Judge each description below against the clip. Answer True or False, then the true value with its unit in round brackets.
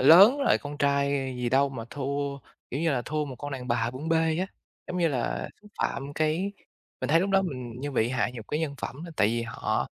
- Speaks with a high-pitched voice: False (140 Hz)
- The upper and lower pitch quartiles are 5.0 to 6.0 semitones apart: False (4.0 semitones)